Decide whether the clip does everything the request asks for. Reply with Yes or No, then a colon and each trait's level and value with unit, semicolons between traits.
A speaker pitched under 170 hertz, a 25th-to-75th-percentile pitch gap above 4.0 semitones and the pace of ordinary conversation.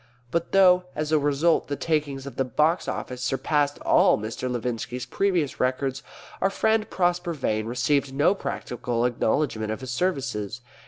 Yes: medium, 140 Hz; average, 4.9 semitones; average, 155 wpm